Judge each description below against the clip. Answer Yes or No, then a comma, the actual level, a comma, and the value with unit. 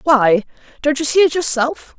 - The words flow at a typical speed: Yes, average, 180 wpm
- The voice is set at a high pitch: Yes, very high, 280 Hz